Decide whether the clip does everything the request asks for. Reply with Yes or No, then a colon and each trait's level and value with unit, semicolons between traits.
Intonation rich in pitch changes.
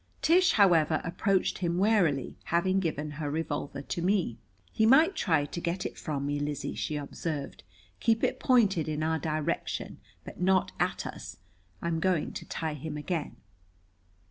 No: average, 4.2 semitones